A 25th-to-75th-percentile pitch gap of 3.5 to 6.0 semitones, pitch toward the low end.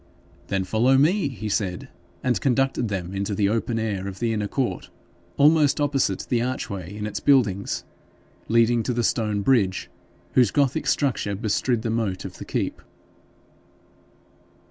Yes: average, 4.6 semitones; low, 115 Hz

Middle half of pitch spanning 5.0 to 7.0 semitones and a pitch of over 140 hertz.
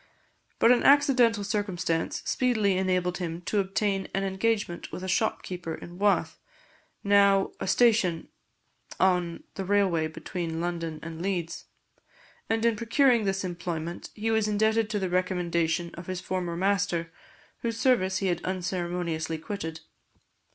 No: average, 3.2 semitones; medium, 185 Hz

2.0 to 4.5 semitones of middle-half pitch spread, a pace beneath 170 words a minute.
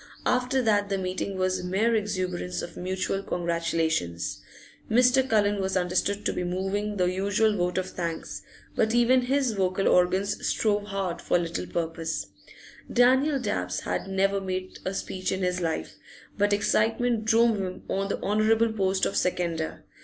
Yes: average, 3.2 semitones; average, 155 wpm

